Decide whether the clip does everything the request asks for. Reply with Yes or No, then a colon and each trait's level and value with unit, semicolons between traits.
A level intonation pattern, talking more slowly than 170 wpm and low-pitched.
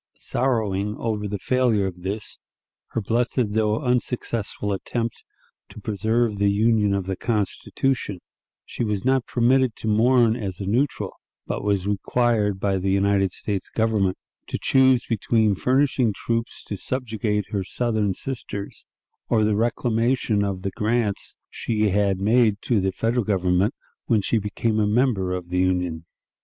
No: average, 3.0 semitones; average, 150 wpm; low, 105 Hz